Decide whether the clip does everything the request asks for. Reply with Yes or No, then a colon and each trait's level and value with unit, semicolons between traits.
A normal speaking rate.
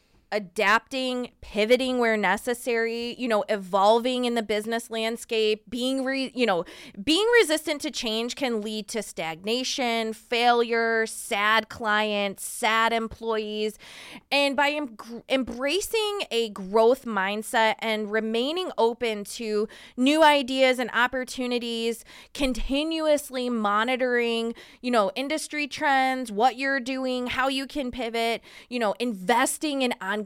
No: slow, 120 wpm